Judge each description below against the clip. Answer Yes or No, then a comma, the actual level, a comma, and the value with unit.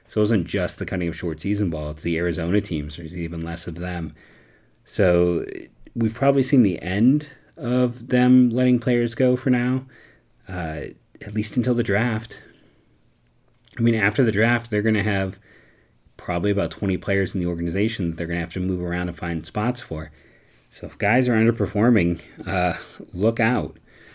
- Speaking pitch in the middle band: No, low, 105 Hz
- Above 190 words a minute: No, average, 185 wpm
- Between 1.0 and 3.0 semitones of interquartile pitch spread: No, wide, 5.6 semitones